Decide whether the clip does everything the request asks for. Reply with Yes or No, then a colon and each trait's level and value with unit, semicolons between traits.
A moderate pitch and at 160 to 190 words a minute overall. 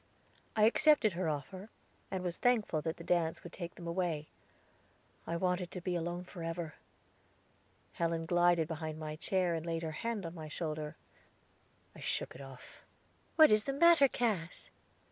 Yes: medium, 175 Hz; average, 165 wpm